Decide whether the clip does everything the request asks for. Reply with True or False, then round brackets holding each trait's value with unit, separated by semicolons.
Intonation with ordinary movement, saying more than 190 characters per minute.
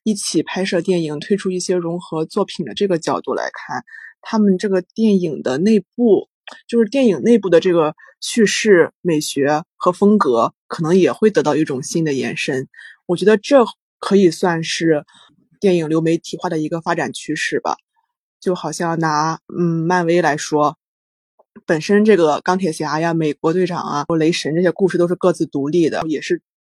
True (4.0 semitones; 265 characters per minute)